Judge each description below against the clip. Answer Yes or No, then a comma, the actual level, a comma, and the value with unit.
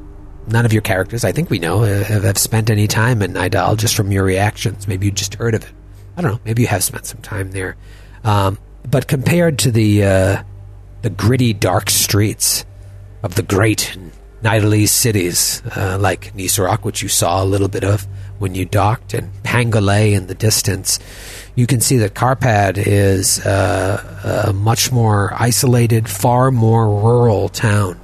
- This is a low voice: Yes, low, 105 Hz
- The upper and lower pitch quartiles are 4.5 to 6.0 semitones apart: No, average, 2.8 semitones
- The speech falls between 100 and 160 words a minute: No, average, 175 wpm